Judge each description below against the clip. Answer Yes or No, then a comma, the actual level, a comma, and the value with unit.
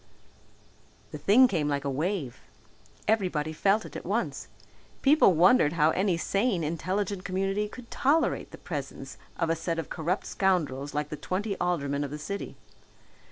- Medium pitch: Yes, medium, 175 Hz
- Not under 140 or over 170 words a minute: Yes, average, 160 wpm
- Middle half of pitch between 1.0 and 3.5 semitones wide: No, average, 4.9 semitones